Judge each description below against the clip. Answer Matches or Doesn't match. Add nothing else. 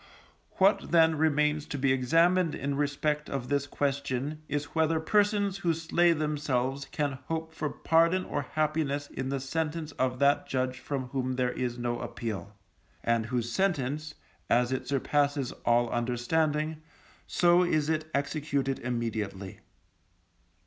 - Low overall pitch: Doesn't match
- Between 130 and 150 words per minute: Matches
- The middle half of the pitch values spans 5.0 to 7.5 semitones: Doesn't match